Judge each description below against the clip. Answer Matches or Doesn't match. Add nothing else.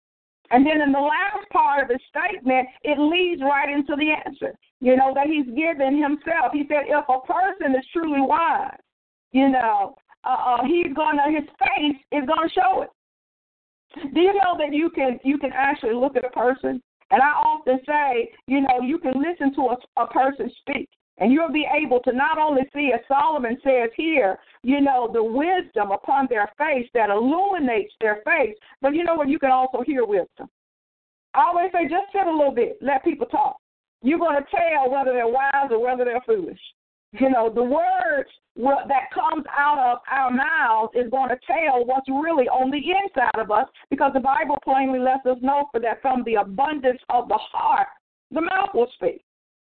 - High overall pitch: Matches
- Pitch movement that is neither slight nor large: Matches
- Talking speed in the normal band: Matches